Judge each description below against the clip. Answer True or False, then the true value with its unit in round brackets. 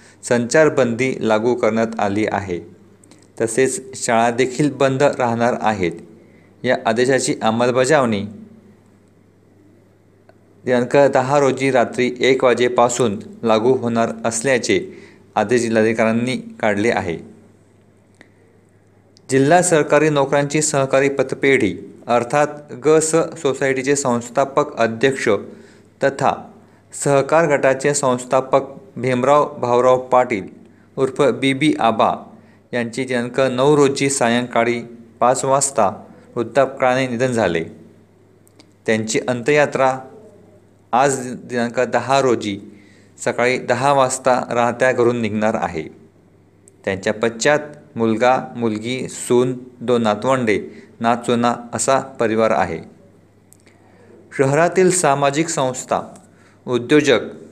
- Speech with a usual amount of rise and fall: True (3.6 semitones)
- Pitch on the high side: False (120 Hz)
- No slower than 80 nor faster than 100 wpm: True (90 wpm)